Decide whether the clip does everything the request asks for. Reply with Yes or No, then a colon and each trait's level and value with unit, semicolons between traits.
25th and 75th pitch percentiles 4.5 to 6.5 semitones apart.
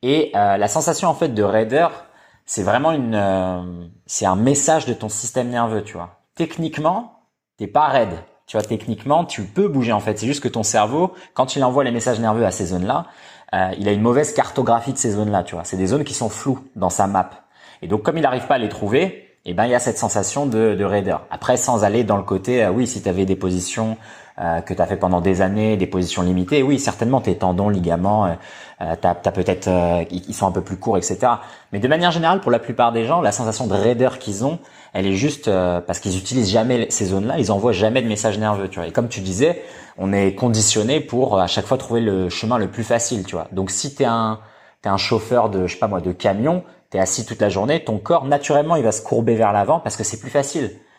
Yes: average, 4.8 semitones